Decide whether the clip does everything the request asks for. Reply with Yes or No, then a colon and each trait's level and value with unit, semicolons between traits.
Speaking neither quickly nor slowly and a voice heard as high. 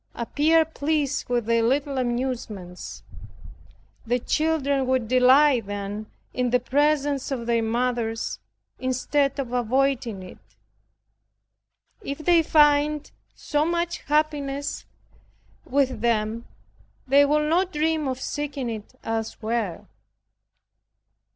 No: slow, 105 wpm; very high, 260 Hz